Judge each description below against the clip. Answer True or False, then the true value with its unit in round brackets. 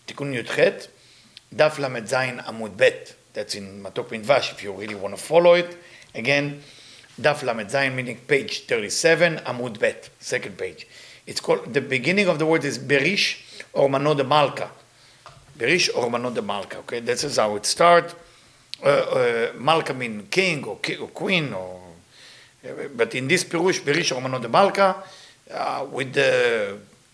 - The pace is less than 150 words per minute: True (140 wpm)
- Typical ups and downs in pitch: False (6.5 semitones)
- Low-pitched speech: False (150 Hz)